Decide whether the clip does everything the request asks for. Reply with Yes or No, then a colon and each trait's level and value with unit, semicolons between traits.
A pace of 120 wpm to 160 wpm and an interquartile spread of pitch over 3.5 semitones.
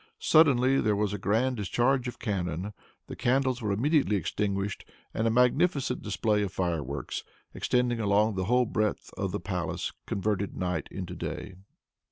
Yes: average, 155 wpm; average, 4.0 semitones